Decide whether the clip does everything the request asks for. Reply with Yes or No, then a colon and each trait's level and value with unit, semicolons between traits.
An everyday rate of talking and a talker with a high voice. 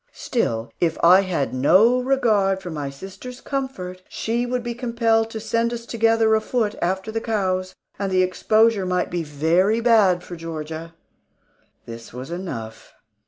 Yes: average, 155 wpm; high, 195 Hz